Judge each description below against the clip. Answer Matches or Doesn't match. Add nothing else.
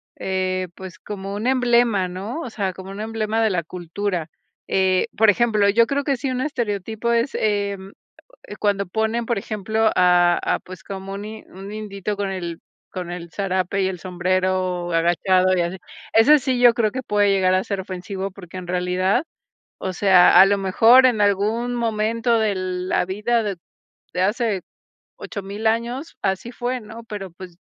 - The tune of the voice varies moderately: Matches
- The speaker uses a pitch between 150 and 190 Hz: Doesn't match